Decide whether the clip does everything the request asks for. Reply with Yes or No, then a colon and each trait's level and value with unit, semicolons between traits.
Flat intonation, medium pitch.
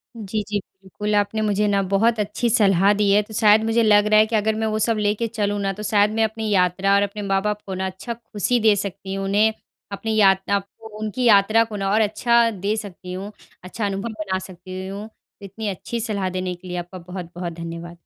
No: narrow, 2.1 semitones; high, 205 Hz